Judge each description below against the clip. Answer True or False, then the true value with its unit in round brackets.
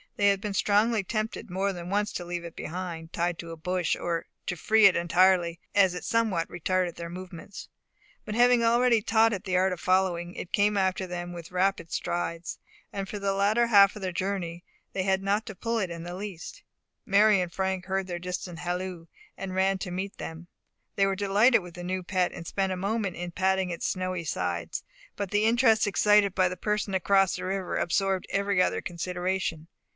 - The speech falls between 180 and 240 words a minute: True (205 wpm)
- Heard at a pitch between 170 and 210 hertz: True (190 Hz)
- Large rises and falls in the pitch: False (2.4 semitones)